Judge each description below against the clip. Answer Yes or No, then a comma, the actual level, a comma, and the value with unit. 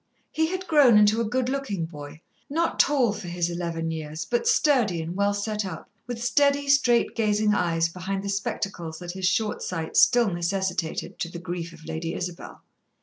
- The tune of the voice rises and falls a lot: Yes, wide, 5.9 semitones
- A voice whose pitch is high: Yes, high, 195 Hz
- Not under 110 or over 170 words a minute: No, average, 185 wpm